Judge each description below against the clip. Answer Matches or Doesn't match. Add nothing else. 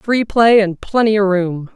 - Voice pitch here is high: Matches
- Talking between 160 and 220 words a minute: Matches